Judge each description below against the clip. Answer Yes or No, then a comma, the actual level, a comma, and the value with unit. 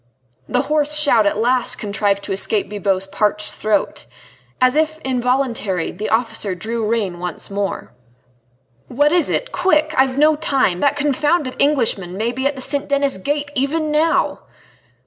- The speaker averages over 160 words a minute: No, average, 155 wpm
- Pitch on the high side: Yes, very high, 255 Hz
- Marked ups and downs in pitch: Yes, wide, 5.9 semitones